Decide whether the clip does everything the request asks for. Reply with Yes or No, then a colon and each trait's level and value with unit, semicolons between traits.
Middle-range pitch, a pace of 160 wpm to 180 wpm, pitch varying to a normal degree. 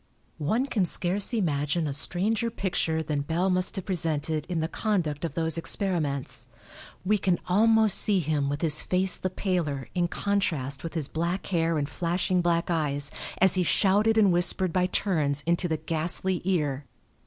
Yes: medium, 175 Hz; average, 170 wpm; average, 3.5 semitones